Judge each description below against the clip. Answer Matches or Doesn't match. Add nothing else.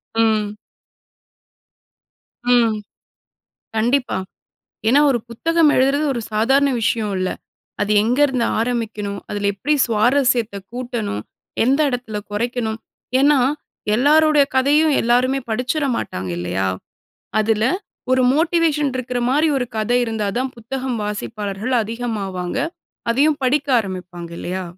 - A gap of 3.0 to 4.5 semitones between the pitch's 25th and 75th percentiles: Matches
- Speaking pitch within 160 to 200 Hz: Doesn't match